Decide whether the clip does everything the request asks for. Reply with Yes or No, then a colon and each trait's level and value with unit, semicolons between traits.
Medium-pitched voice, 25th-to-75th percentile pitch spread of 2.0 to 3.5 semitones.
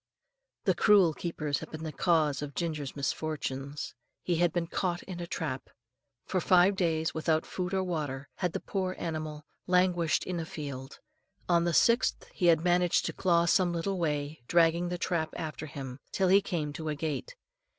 Yes: medium, 165 Hz; average, 2.8 semitones